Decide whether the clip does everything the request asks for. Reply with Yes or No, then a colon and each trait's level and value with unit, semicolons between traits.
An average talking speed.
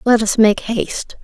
Yes: average, 195 wpm